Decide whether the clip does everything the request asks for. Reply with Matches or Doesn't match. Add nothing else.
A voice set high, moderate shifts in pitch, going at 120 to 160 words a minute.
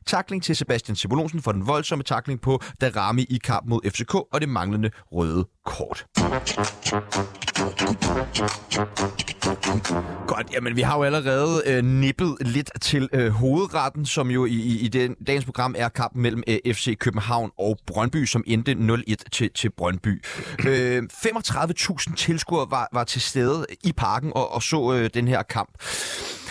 Doesn't match